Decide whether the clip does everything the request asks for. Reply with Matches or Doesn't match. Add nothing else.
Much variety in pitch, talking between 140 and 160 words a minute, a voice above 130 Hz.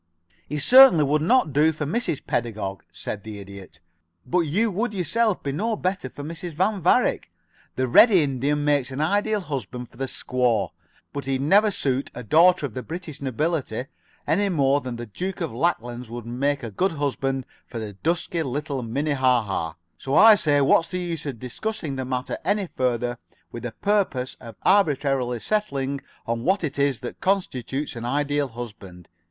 Doesn't match